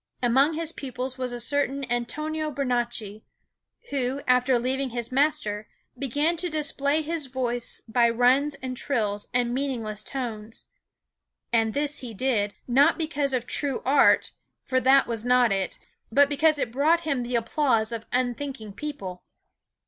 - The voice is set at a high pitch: Yes, very high, 255 Hz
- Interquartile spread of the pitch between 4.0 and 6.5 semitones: No, average, 3.3 semitones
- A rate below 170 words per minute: Yes, average, 150 wpm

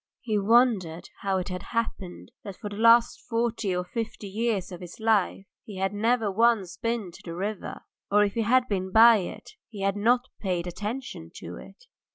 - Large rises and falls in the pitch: No, average, 3.5 semitones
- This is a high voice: Yes, high, 210 Hz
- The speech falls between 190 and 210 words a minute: Yes, average, 195 wpm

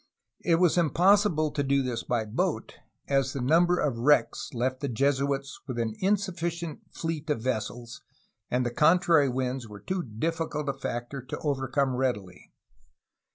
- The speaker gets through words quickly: No, average, 155 wpm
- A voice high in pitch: No, medium, 140 Hz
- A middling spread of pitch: Yes, average, 4.8 semitones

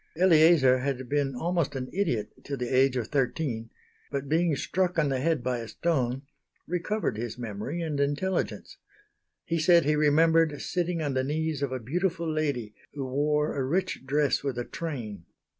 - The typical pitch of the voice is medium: Yes, medium, 145 Hz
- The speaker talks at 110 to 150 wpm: No, average, 175 wpm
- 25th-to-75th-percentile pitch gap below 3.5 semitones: No, average, 4.2 semitones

